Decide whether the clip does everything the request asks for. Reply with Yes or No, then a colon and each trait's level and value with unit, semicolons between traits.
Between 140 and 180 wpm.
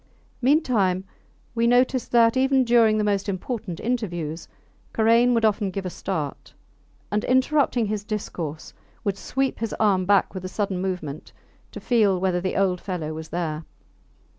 Yes: average, 155 wpm